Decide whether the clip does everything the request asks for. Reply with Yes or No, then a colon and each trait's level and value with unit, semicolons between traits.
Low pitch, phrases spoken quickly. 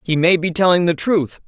No: medium, 170 Hz; fast, 245 wpm